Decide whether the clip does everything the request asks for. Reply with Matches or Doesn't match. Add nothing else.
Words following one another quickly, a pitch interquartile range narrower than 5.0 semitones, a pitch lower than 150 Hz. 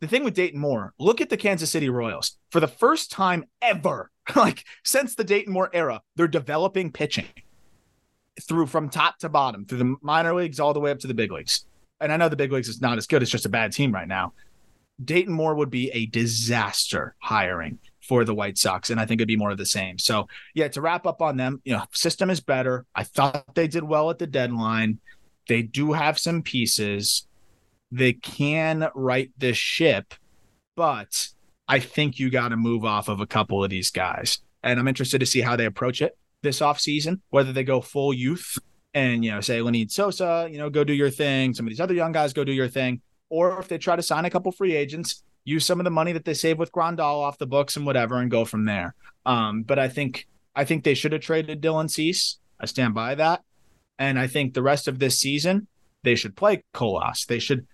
Doesn't match